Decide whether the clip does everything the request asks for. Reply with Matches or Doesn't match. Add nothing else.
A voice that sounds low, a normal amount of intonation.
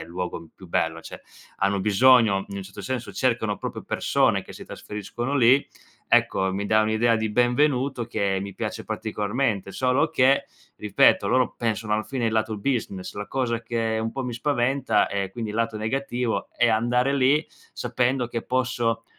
Matches